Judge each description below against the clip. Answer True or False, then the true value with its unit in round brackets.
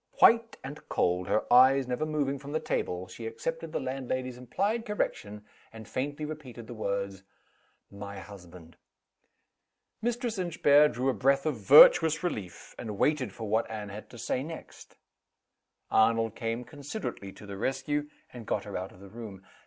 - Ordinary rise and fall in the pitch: False (6.3 semitones)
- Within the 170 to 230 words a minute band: False (160 wpm)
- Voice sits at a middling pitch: False (125 Hz)